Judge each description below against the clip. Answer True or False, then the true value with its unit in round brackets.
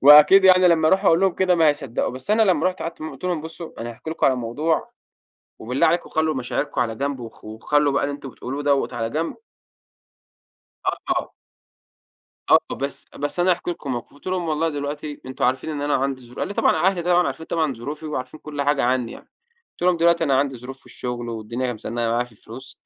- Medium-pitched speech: True (145 Hz)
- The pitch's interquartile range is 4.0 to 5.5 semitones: True (4.5 semitones)